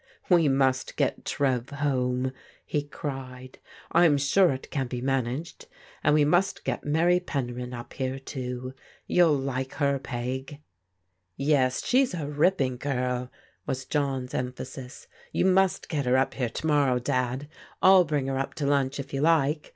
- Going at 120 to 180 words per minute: Yes, average, 170 wpm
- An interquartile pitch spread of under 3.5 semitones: Yes, narrow, 2.6 semitones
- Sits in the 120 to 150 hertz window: Yes, low, 135 Hz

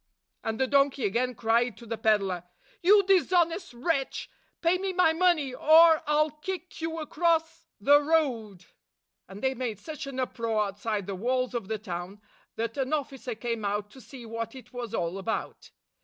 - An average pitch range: No, wide, 6.2 semitones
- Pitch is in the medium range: No, very high, 255 Hz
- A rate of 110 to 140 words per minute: No, average, 185 wpm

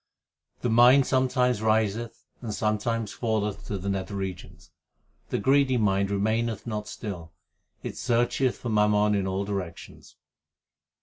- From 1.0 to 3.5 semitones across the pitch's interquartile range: Yes, average, 2.9 semitones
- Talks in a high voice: No, low, 105 Hz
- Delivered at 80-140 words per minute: Yes, slow, 135 wpm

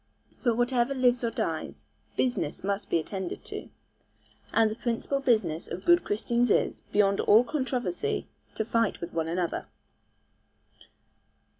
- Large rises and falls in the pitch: No, average, 4.2 semitones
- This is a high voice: Yes, high, 230 Hz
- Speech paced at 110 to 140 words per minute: Yes, slow, 135 wpm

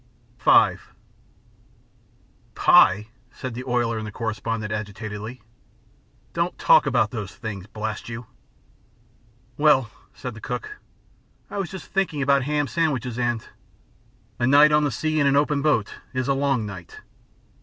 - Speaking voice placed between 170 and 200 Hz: No, low, 125 Hz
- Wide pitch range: No, average, 4.8 semitones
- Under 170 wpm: Yes, average, 145 wpm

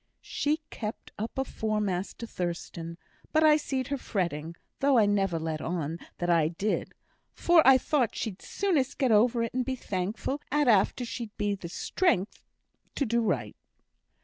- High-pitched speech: Yes, high, 220 Hz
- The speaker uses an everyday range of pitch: No, wide, 6.6 semitones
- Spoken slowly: No, average, 160 wpm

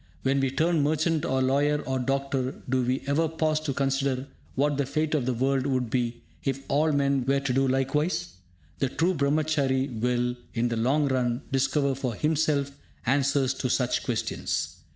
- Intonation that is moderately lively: No, narrow, 2.2 semitones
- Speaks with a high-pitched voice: No, low, 135 Hz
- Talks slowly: No, average, 175 wpm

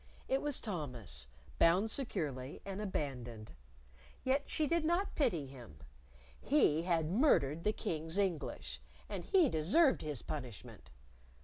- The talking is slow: Yes, slow, 125 wpm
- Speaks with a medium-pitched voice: Yes, medium, 170 Hz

